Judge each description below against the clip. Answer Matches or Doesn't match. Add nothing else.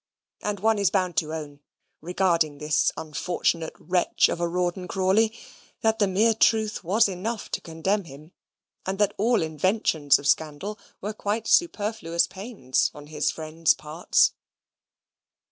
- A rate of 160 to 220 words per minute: Doesn't match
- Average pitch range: Matches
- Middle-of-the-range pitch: Matches